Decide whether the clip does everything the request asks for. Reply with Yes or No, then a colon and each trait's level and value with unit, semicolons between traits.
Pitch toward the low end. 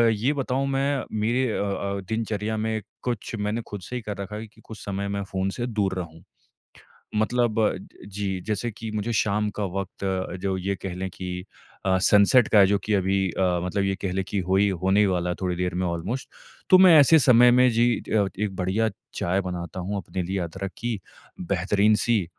Yes: low, 100 Hz